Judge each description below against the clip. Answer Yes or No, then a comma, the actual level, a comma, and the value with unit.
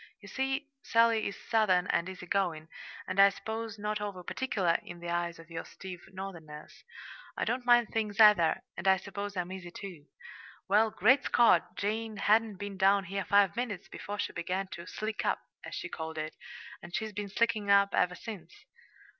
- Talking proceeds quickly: No, average, 185 wpm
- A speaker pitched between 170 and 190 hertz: No, high, 200 Hz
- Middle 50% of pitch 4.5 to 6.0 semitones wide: No, average, 3.4 semitones